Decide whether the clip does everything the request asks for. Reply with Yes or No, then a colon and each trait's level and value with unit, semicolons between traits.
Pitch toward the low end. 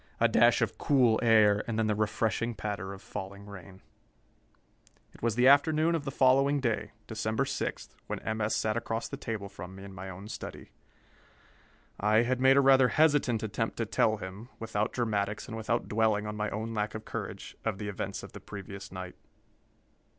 Yes: low, 110 Hz